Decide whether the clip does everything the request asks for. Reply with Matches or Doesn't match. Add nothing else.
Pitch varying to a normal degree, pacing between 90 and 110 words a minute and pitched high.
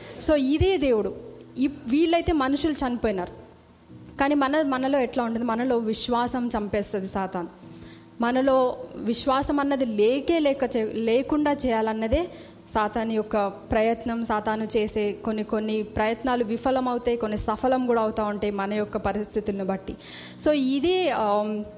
Doesn't match